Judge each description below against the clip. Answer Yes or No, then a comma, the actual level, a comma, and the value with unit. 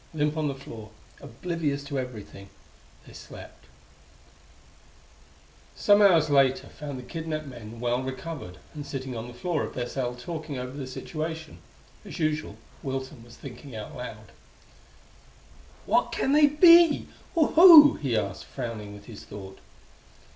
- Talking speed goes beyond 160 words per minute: No, average, 145 wpm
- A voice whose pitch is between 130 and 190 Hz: Yes, low, 135 Hz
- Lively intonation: No, average, 5.0 semitones